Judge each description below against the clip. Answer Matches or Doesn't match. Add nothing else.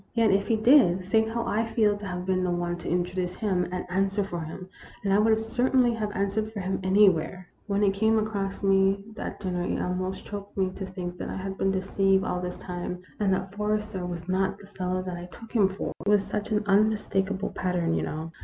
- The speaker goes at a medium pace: Doesn't match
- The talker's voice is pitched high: Matches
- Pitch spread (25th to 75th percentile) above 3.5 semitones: Doesn't match